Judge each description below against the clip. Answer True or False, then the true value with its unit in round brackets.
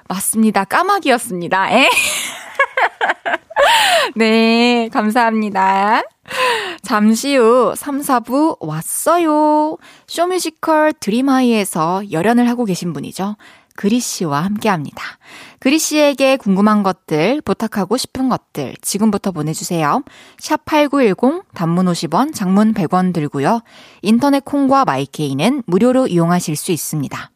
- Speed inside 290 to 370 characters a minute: False (245 characters per minute)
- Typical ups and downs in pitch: False (6.7 semitones)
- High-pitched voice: True (225 Hz)